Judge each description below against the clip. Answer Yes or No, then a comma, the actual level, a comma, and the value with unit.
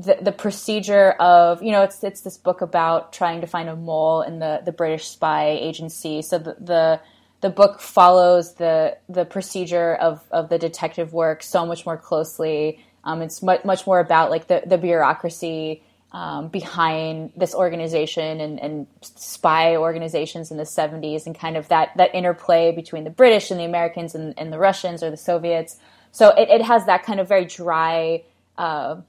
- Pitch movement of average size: No, narrow, 2.3 semitones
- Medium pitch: Yes, medium, 165 Hz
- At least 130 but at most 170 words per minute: No, average, 185 wpm